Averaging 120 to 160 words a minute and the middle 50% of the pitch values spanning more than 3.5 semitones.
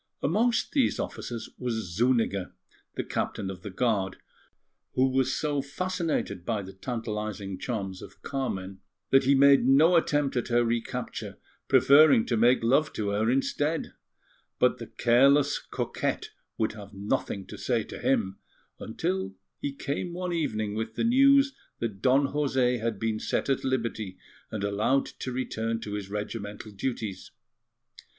Yes: average, 150 wpm; average, 5.1 semitones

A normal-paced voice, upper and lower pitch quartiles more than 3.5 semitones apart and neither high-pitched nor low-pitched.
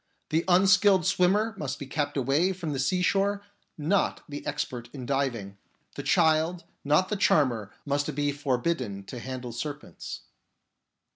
Yes: average, 150 wpm; wide, 5.5 semitones; medium, 145 Hz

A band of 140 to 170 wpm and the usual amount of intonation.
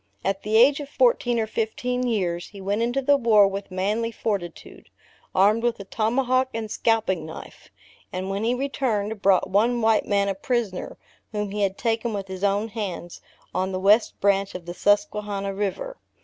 No: average, 180 wpm; average, 3.0 semitones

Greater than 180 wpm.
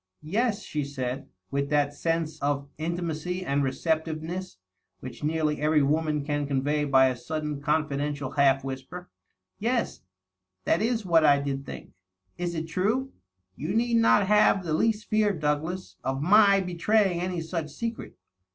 No: average, 160 wpm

